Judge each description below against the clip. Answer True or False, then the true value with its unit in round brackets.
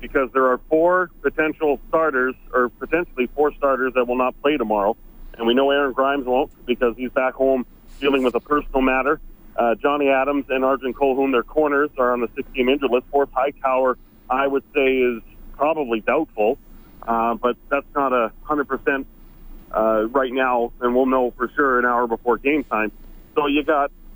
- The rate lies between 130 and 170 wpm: False (185 wpm)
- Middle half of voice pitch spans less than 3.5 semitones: True (2.4 semitones)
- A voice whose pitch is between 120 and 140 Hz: True (130 Hz)